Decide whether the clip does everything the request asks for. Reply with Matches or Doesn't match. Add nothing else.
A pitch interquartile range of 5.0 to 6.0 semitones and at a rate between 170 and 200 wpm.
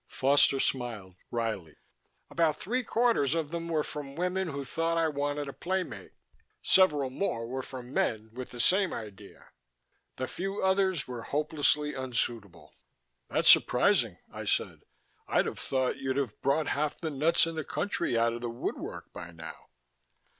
Doesn't match